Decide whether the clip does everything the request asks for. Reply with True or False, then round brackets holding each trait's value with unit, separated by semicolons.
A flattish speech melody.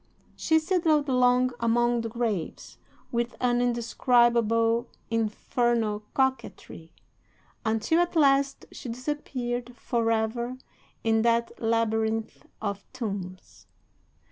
True (2.0 semitones)